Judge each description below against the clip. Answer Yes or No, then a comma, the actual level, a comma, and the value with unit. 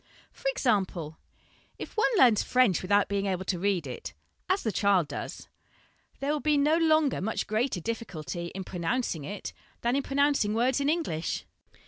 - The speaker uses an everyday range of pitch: No, wide, 7.2 semitones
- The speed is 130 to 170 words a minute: Yes, average, 165 wpm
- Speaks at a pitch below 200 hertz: No, high, 215 Hz